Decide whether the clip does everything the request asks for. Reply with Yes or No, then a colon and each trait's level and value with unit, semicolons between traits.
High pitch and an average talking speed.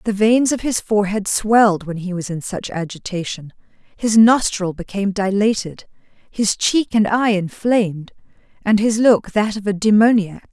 Yes: high, 205 Hz; average, 155 wpm